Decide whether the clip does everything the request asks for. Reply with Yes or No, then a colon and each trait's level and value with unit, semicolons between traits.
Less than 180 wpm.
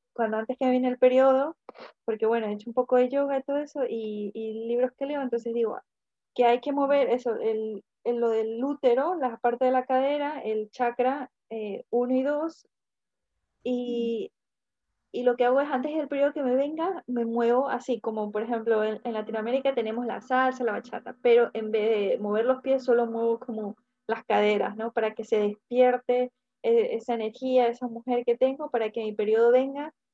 No: average, 195 wpm